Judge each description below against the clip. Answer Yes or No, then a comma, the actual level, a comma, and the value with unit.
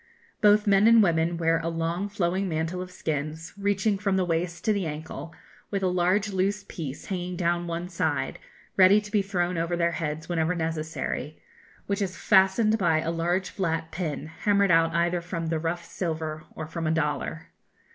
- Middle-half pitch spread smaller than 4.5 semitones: Yes, average, 2.8 semitones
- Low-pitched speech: No, medium, 175 Hz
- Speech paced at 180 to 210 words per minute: Yes, average, 185 wpm